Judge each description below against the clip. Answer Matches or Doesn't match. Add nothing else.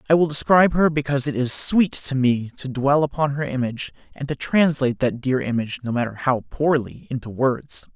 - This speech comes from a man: Matches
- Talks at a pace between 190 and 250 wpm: Matches